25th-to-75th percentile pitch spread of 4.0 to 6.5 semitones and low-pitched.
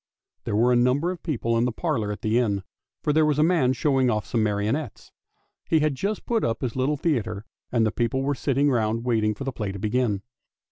Yes: average, 4.8 semitones; low, 125 Hz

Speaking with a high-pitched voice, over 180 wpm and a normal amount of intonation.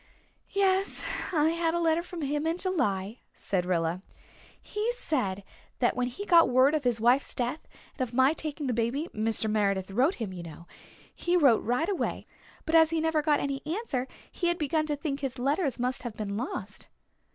No: very high, 275 Hz; average, 195 wpm; wide, 5.8 semitones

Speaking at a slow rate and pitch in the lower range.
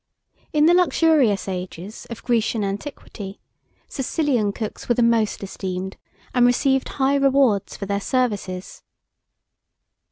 No: slow, 120 wpm; high, 230 Hz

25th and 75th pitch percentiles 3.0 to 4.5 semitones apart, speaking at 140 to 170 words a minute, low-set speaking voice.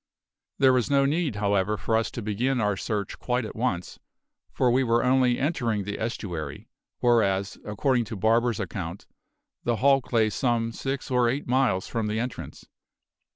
Yes: average, 3.6 semitones; average, 165 wpm; low, 115 Hz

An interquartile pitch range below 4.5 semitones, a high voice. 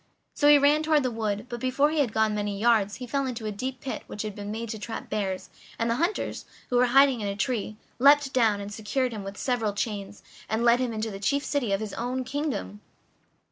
Yes: average, 3.9 semitones; high, 230 Hz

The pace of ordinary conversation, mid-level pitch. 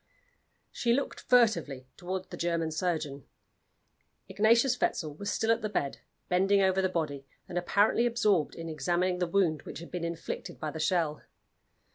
Yes: average, 160 wpm; medium, 180 Hz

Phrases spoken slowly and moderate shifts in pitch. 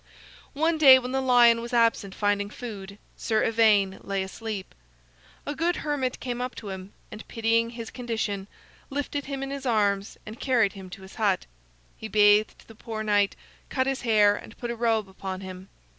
No: average, 185 wpm; average, 3.6 semitones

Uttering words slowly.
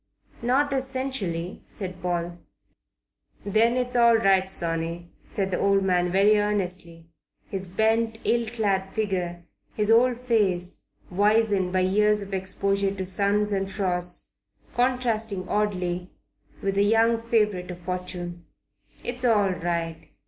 Yes: slow, 125 wpm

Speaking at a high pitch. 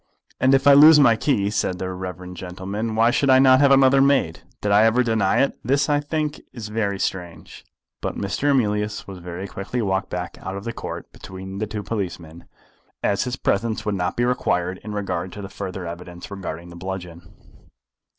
No: low, 100 Hz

